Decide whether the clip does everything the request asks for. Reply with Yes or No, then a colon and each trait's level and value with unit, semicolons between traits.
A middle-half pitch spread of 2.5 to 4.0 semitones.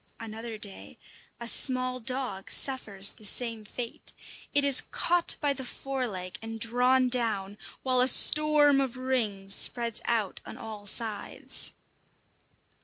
Yes: average, 3.4 semitones